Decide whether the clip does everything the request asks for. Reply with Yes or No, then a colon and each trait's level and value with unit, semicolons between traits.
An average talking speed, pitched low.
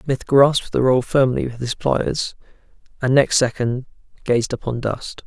Yes: average, 160 wpm; low, 130 Hz